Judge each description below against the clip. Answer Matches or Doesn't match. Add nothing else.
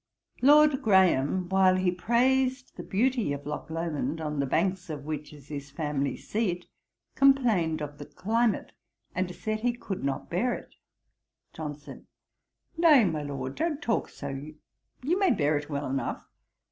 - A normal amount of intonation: Doesn't match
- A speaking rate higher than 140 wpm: Matches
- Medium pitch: Matches